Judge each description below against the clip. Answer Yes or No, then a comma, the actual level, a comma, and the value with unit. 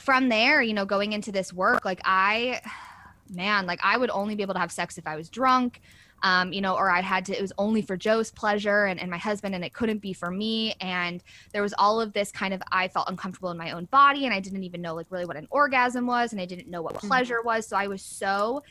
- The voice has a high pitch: Yes, high, 200 Hz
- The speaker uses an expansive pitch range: No, average, 3.4 semitones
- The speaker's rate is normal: No, fast, 270 wpm